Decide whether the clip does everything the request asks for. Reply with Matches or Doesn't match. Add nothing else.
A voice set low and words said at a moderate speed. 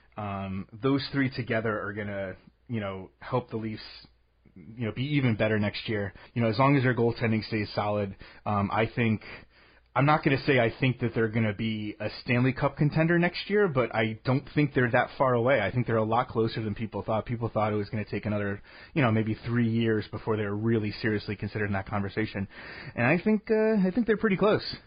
Doesn't match